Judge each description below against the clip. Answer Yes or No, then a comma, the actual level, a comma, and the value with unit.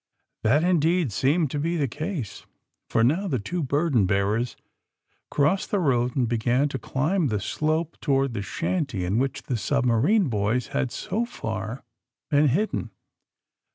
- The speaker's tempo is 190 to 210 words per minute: No, average, 160 wpm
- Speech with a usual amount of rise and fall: No, wide, 5.8 semitones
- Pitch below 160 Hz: Yes, low, 135 Hz